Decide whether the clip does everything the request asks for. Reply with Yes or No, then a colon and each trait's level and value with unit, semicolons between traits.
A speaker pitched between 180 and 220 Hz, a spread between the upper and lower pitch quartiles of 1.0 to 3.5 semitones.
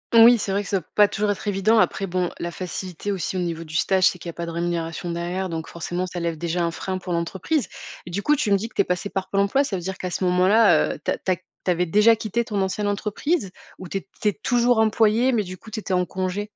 Yes: high, 190 Hz; average, 3.1 semitones